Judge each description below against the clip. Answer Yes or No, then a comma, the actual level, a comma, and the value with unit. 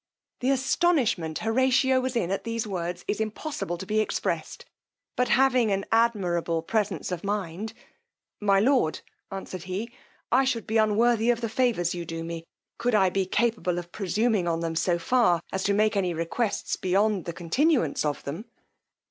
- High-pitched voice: Yes, high, 210 Hz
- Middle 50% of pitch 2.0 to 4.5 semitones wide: No, average, 5.2 semitones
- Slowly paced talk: No, average, 170 wpm